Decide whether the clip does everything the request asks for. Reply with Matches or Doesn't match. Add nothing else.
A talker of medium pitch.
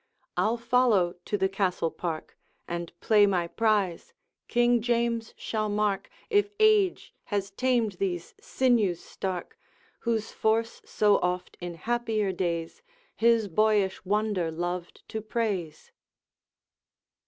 Doesn't match